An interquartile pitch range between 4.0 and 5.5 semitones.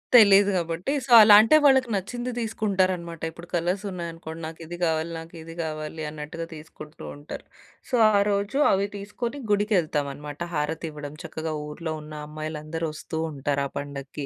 Yes: average, 4.4 semitones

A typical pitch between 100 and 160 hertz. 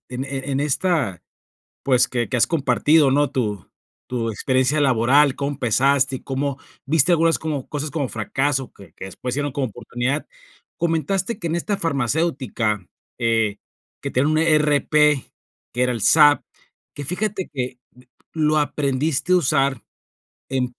Yes: medium, 140 Hz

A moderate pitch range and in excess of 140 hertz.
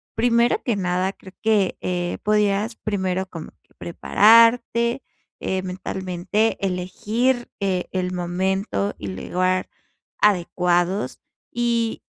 Yes: average, 3.5 semitones; high, 190 Hz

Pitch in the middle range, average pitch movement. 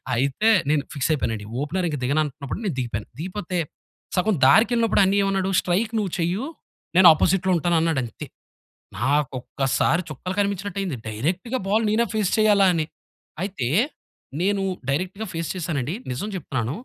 No: medium, 175 Hz; wide, 6.0 semitones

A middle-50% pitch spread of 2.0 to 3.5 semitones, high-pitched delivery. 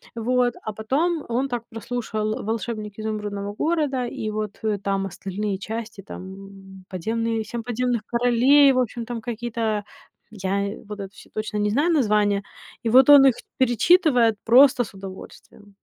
Yes: average, 3.1 semitones; high, 220 Hz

